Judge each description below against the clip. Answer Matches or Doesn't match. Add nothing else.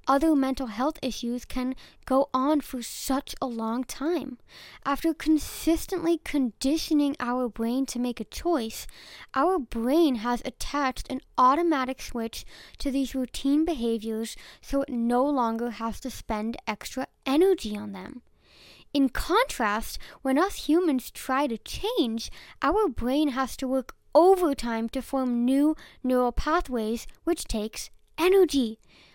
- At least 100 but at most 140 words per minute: Matches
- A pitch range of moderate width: Matches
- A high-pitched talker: Matches